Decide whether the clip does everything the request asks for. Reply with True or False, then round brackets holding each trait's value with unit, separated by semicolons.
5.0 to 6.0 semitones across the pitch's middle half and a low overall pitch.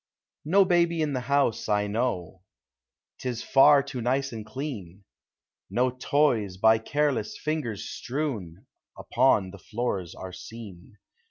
True (5.6 semitones; 120 Hz)